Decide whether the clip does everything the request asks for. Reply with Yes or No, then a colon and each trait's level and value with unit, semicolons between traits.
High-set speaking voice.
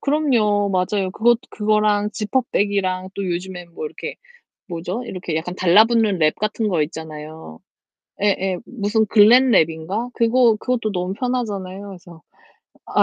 Yes: high, 200 Hz